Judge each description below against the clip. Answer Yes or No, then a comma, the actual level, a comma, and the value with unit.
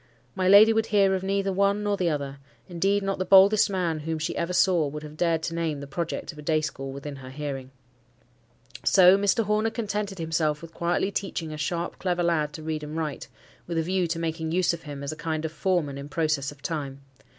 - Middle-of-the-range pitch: Yes, medium, 165 Hz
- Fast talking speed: Yes, fast, 230 wpm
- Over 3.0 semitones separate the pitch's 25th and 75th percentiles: Yes, average, 4.0 semitones